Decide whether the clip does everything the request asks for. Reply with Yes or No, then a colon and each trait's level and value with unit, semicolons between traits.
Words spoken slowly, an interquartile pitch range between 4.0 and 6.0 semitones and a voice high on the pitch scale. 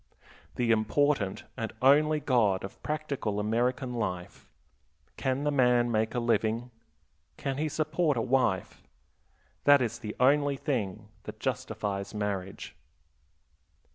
No: slow, 120 wpm; average, 4.9 semitones; low, 120 Hz